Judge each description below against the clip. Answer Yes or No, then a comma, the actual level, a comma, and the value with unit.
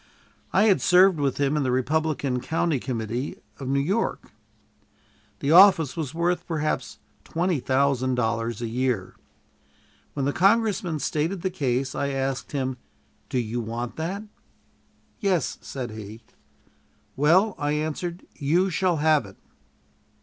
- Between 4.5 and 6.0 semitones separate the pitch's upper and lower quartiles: Yes, average, 5.2 semitones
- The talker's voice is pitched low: No, medium, 145 Hz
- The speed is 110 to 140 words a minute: Yes, slow, 135 wpm